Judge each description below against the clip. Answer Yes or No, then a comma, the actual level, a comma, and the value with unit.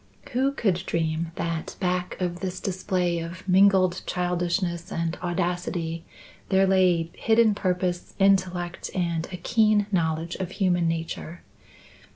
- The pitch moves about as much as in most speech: No, narrow, 1.9 semitones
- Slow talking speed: Yes, slow, 125 wpm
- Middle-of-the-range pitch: Yes, medium, 180 Hz